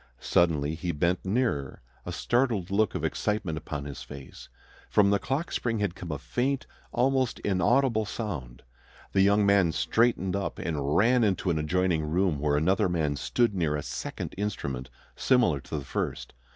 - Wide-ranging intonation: Yes, wide, 6.2 semitones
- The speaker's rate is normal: Yes, average, 165 wpm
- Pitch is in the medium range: No, very low, 95 Hz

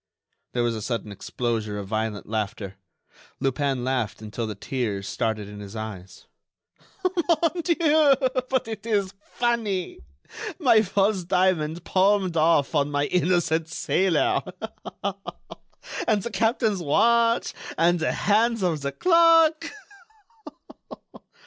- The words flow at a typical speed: No, slow, 115 wpm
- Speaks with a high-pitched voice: No, medium, 170 Hz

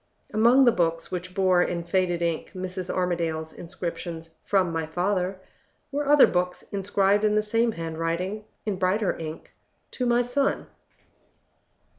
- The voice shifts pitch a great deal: No, average, 3.7 semitones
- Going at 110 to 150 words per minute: Yes, average, 140 wpm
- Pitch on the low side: No, medium, 185 Hz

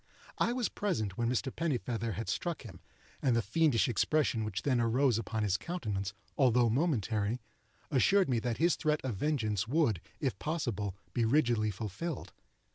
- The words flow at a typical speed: Yes, average, 160 wpm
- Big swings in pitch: Yes, wide, 5.9 semitones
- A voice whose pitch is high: No, low, 120 Hz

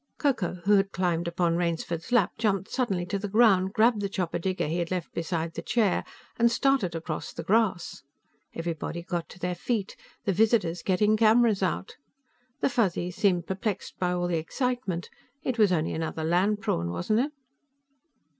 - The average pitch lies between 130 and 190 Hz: Yes, medium, 185 Hz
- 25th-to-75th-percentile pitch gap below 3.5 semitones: No, average, 3.9 semitones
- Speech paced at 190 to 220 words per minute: No, average, 175 wpm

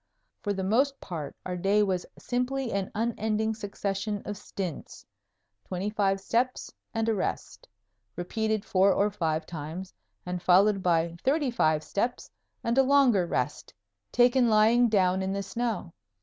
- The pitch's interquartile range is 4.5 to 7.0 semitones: No, average, 3.9 semitones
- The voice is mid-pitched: No, high, 205 Hz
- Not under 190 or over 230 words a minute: No, average, 150 wpm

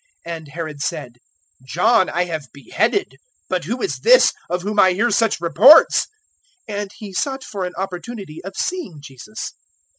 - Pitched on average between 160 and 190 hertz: Yes, medium, 185 Hz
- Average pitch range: No, wide, 5.7 semitones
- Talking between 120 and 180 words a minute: Yes, average, 160 wpm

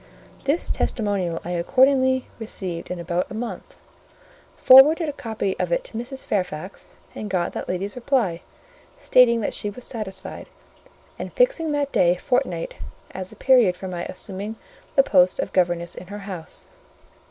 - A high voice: Yes, high, 205 Hz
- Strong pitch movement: Yes, wide, 6.2 semitones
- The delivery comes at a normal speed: Yes, average, 155 wpm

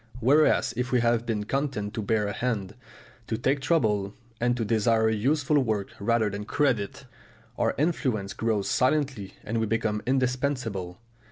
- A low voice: Yes, low, 115 Hz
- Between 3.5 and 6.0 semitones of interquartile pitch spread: Yes, average, 3.8 semitones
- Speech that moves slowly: No, average, 155 wpm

